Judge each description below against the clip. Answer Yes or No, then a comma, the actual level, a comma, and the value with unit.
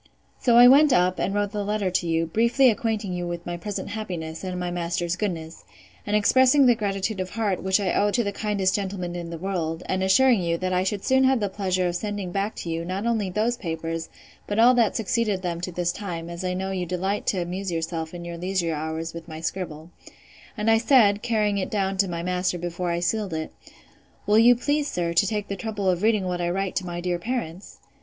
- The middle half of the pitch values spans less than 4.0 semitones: Yes, average, 3.4 semitones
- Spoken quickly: Yes, fast, 235 wpm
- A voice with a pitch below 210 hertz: Yes, high, 190 Hz